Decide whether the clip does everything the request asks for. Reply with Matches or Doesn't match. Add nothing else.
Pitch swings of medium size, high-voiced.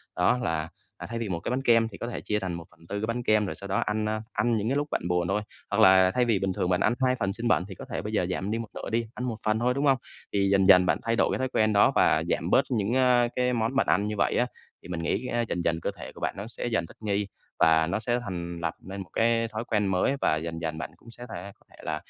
Doesn't match